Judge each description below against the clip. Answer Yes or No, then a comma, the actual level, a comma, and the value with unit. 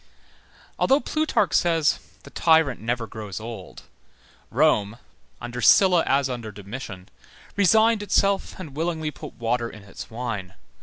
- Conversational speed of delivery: No, slow, 130 wpm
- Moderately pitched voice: No, low, 125 Hz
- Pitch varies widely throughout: Yes, wide, 7.3 semitones